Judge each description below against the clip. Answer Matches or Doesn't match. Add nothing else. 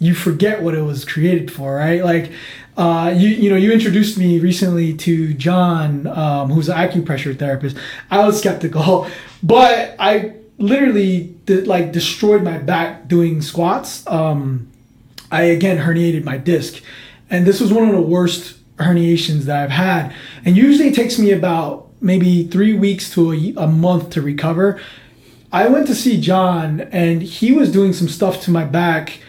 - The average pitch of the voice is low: Doesn't match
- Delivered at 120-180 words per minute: Matches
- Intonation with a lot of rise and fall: Doesn't match